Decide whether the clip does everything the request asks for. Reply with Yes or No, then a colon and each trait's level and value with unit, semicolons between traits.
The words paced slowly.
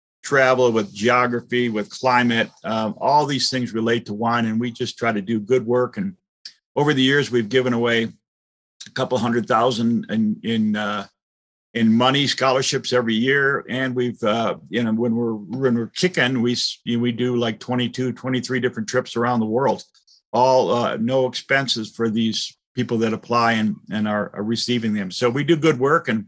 No: average, 185 wpm